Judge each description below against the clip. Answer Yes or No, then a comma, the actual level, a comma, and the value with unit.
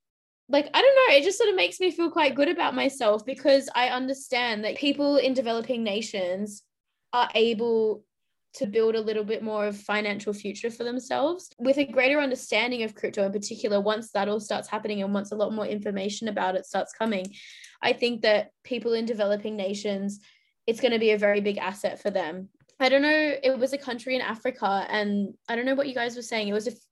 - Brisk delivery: Yes, fast, 220 wpm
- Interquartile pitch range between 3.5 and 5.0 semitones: Yes, average, 4.1 semitones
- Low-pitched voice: No, high, 230 Hz